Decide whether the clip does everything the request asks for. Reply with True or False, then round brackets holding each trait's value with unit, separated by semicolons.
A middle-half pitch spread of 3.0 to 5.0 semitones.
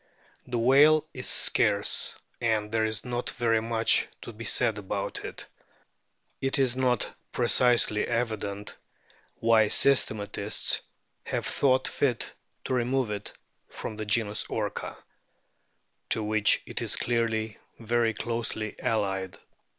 False (2.4 semitones)